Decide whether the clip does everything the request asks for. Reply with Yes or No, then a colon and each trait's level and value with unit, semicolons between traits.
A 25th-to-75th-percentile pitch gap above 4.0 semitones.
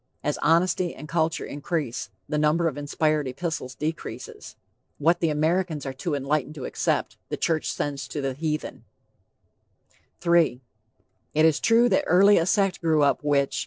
No: average, 2.8 semitones